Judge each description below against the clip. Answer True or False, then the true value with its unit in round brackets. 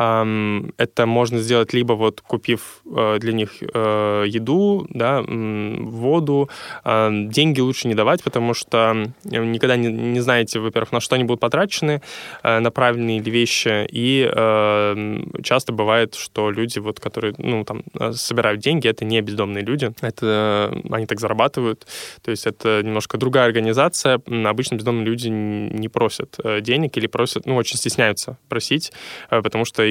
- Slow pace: False (140 wpm)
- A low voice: True (115 Hz)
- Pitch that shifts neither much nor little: False (2.3 semitones)